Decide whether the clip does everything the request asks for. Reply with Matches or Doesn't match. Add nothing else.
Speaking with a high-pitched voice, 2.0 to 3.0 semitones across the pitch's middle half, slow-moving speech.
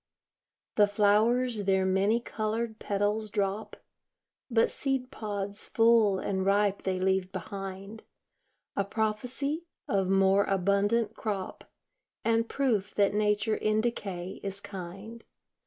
Matches